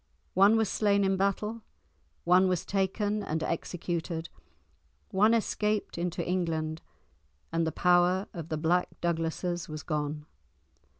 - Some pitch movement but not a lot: Yes, average, 3.3 semitones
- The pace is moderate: No, slow, 125 wpm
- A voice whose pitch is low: No, medium, 180 Hz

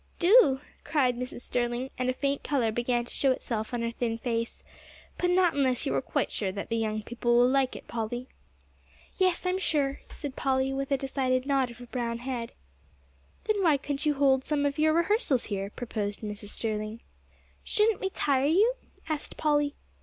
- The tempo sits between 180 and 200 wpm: Yes, average, 190 wpm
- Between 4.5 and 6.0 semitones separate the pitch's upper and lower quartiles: No, average, 3.6 semitones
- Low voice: No, very high, 260 Hz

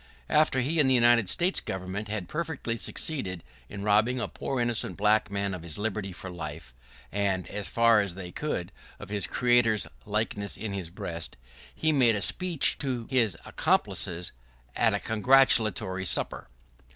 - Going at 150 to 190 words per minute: Yes, average, 165 wpm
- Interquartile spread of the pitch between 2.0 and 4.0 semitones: No, average, 4.5 semitones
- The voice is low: Yes, low, 105 Hz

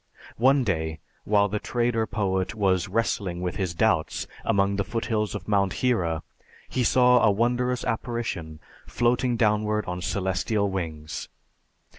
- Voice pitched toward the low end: Yes, low, 105 Hz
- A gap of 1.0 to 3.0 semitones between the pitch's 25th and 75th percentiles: No, average, 4.1 semitones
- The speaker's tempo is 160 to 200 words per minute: No, slow, 135 wpm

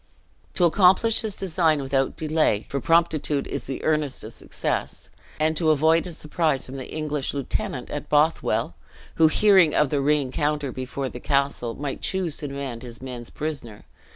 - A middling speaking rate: Yes, average, 165 wpm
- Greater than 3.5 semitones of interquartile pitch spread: No, average, 2.9 semitones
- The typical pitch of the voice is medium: Yes, medium, 150 Hz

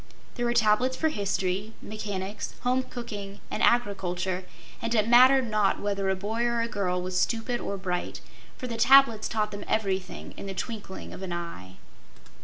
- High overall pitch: Yes, high, 210 Hz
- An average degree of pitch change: Yes, average, 3.7 semitones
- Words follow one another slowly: No, average, 175 wpm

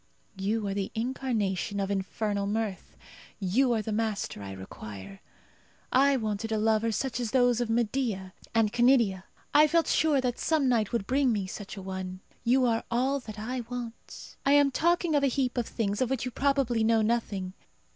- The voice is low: No, high, 225 Hz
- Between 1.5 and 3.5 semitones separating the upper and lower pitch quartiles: No, average, 4.2 semitones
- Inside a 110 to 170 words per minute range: No, average, 185 wpm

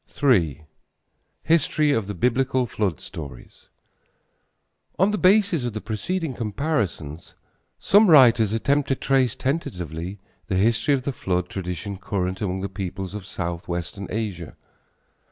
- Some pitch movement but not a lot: No, wide, 6.8 semitones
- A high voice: No, low, 105 Hz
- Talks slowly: Yes, slow, 130 wpm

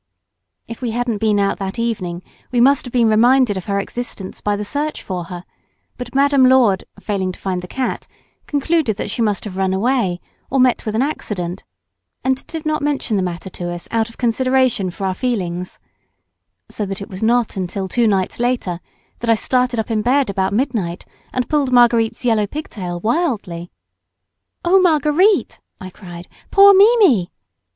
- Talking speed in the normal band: Yes, average, 180 wpm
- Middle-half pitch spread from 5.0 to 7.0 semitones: Yes, average, 5.3 semitones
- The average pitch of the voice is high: Yes, high, 225 Hz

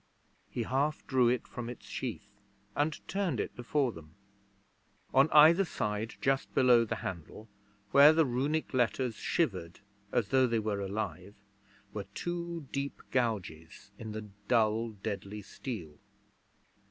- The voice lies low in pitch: Yes, low, 120 Hz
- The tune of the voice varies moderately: Yes, average, 4.7 semitones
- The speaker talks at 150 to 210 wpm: No, slow, 135 wpm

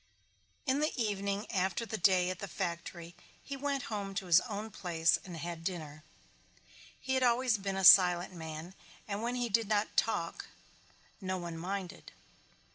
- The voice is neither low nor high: No, high, 195 Hz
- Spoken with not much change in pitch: No, average, 4.1 semitones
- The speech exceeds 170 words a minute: No, average, 165 wpm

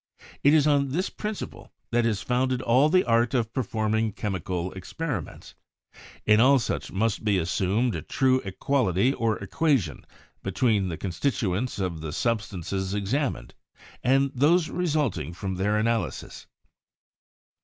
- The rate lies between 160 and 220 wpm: No, average, 140 wpm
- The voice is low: Yes, low, 115 Hz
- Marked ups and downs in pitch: Yes, wide, 5.7 semitones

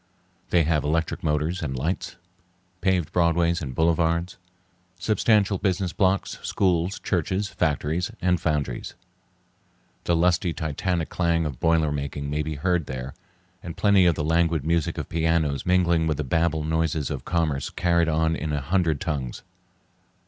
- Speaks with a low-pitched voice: Yes, very low, 80 Hz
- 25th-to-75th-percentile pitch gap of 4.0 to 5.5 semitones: No, narrow, 2.6 semitones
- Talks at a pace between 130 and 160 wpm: Yes, average, 150 wpm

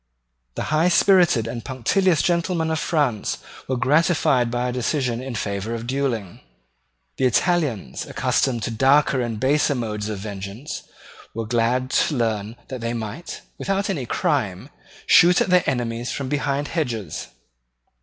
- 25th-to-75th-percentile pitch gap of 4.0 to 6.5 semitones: Yes, average, 4.7 semitones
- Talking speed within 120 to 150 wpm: Yes, average, 145 wpm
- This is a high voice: No, low, 125 Hz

